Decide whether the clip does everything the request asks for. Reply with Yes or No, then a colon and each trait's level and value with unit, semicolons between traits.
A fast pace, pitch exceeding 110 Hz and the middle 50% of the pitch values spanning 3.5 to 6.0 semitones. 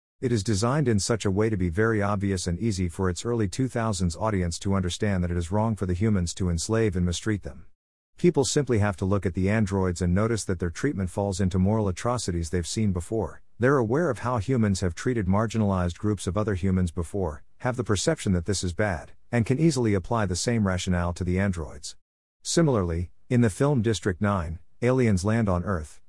No: fast, 210 wpm; low, 100 Hz; average, 4.0 semitones